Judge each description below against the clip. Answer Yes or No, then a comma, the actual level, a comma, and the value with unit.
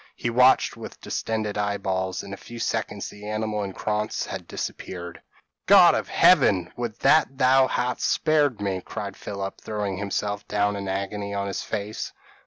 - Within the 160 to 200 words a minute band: Yes, average, 170 wpm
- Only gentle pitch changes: Yes, narrow, 2.2 semitones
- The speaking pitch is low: Yes, low, 105 Hz